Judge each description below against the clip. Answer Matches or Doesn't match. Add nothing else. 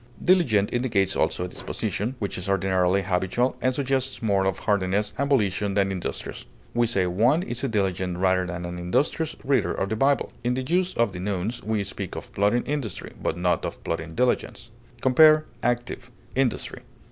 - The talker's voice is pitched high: Doesn't match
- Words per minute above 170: Matches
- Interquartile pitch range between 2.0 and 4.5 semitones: Doesn't match